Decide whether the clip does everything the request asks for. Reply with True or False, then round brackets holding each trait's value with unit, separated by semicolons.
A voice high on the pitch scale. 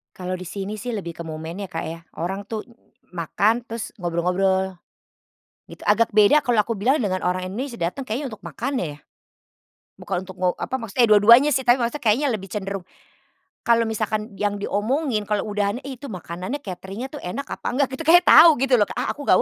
True (210 Hz)